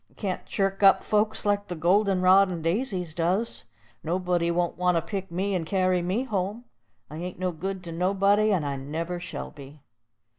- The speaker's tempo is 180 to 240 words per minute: Yes, average, 190 wpm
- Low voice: No, medium, 185 Hz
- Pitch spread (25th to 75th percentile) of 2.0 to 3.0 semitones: Yes, narrow, 2.6 semitones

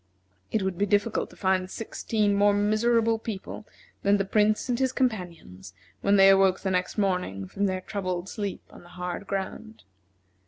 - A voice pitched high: Yes, high, 200 Hz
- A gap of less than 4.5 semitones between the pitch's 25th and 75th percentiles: Yes, narrow, 2.5 semitones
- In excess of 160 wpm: Yes, average, 170 wpm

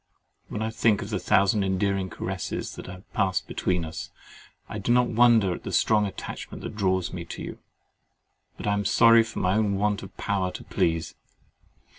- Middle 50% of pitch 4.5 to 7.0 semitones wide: No, average, 2.8 semitones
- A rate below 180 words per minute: No, average, 190 wpm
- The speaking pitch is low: Yes, low, 100 Hz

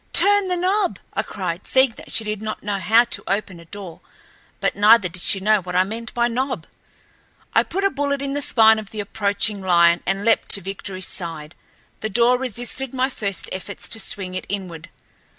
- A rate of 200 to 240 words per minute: Yes, fast, 205 wpm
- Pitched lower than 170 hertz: No, high, 210 Hz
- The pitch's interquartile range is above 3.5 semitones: Yes, average, 4.4 semitones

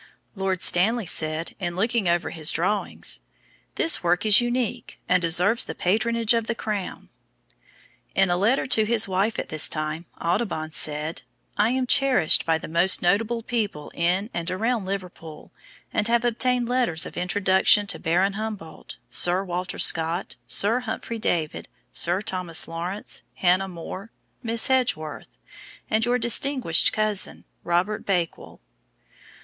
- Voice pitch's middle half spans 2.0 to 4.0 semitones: No, average, 4.8 semitones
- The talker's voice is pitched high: Yes, high, 195 Hz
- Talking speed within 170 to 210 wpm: No, average, 145 wpm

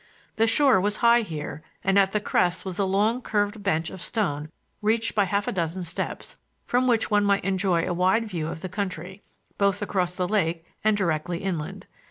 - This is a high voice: Yes, high, 195 Hz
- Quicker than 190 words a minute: Yes, average, 200 wpm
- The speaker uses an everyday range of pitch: Yes, average, 3.2 semitones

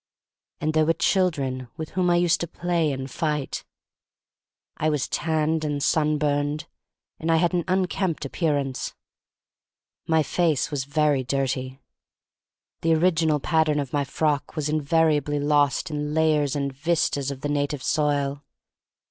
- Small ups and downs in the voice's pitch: Yes, narrow, 2.2 semitones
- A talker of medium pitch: Yes, medium, 150 Hz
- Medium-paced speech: Yes, average, 145 wpm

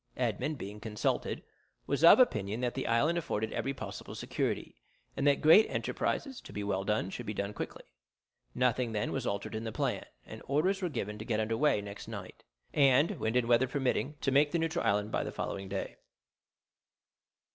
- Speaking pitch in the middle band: No, low, 120 Hz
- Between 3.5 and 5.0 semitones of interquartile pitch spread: No, wide, 5.6 semitones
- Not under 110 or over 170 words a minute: No, average, 190 wpm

